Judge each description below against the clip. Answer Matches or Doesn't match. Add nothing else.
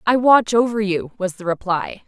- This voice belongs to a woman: Matches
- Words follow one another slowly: Doesn't match